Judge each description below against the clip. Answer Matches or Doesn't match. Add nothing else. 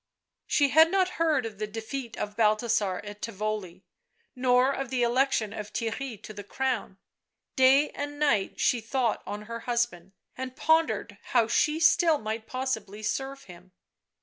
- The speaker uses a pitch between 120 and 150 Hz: Doesn't match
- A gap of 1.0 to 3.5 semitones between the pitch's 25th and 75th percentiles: Doesn't match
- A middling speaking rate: Matches